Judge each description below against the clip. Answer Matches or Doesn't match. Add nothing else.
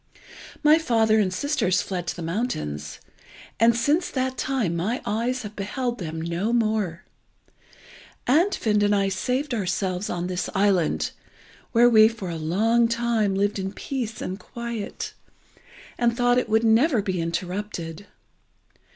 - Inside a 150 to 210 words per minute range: Doesn't match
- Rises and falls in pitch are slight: Doesn't match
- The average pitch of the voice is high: Matches